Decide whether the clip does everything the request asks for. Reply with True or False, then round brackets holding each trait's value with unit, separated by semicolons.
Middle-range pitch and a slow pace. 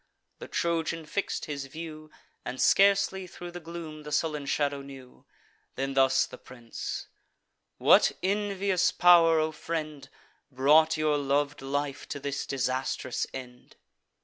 True (150 Hz; 130 wpm)